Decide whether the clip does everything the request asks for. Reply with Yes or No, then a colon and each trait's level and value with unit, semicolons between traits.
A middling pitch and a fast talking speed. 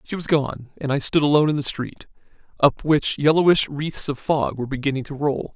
Yes: medium, 145 Hz; fast, 215 wpm